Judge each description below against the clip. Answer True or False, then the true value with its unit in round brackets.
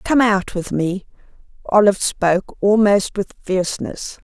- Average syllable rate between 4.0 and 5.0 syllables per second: True (4.4 syllables/s)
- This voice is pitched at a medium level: False (195 Hz)